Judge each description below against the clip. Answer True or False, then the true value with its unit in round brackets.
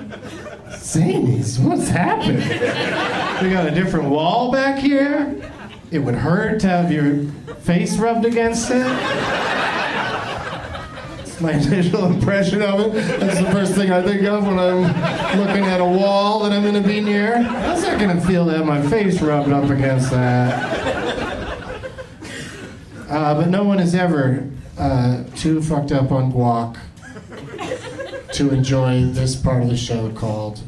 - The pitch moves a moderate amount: False (6.7 semitones)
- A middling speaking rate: True (155 wpm)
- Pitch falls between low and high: True (170 Hz)